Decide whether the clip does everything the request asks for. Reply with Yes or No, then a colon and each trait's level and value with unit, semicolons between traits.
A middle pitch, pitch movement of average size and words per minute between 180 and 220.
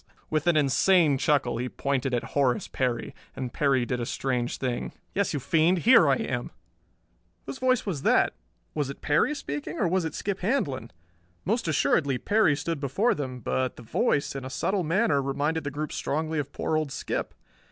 Yes: medium, 145 Hz; average, 4.4 semitones; average, 185 wpm